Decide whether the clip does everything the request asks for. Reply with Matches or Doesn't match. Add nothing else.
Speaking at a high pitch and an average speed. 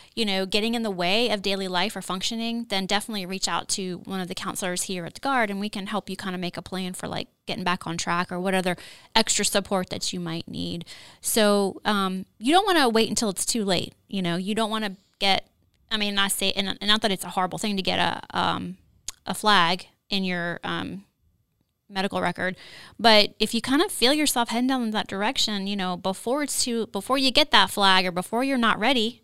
Doesn't match